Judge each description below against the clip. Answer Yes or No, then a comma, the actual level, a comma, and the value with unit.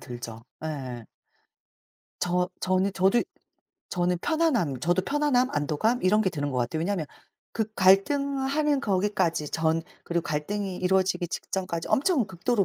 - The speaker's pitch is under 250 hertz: Yes, medium, 185 Hz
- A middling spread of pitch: No, wide, 5.7 semitones